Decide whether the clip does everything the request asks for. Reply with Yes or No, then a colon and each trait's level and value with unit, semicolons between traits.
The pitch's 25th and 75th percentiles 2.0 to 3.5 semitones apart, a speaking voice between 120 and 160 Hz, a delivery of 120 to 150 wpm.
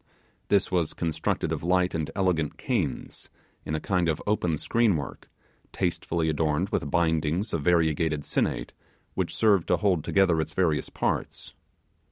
No: average, 2.9 semitones; very low, 85 Hz; average, 145 wpm